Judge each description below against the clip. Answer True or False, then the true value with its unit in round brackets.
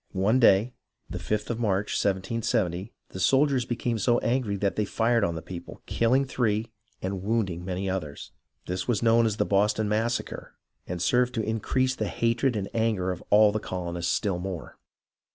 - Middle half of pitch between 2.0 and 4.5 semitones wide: True (3.8 semitones)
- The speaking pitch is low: True (105 Hz)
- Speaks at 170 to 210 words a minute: True (180 wpm)